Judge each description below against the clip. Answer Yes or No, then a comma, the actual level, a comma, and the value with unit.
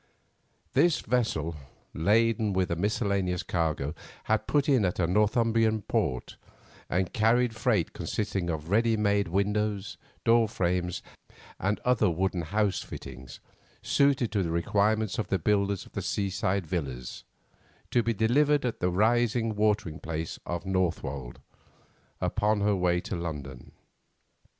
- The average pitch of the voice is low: Yes, low, 100 Hz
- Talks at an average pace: No, slow, 130 wpm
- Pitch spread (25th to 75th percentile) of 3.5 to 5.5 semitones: Yes, average, 4.3 semitones